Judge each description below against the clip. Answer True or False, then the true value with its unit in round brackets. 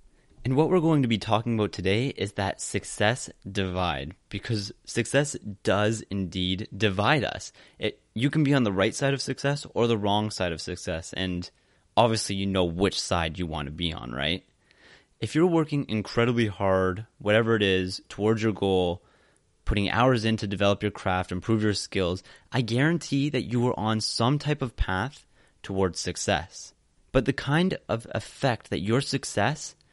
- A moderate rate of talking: True (175 wpm)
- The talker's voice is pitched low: True (105 Hz)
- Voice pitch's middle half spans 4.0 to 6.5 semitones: True (5.1 semitones)